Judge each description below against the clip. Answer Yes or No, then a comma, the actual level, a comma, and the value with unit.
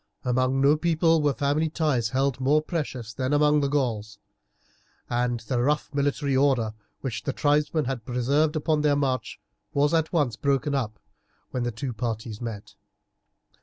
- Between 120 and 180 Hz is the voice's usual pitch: Yes, medium, 140 Hz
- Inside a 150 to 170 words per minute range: Yes, average, 160 wpm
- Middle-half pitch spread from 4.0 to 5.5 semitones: No, average, 3.5 semitones